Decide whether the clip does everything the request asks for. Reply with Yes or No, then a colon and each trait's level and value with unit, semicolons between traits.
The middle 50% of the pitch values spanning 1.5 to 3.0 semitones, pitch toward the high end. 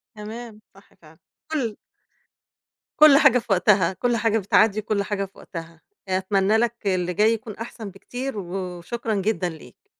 No: average, 3.4 semitones; high, 210 Hz